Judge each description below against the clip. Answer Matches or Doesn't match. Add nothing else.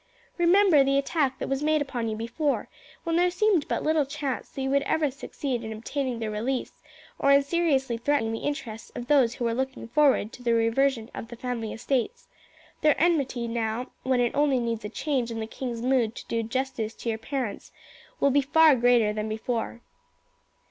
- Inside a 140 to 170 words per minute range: Doesn't match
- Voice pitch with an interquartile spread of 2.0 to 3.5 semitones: Doesn't match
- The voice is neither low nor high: Doesn't match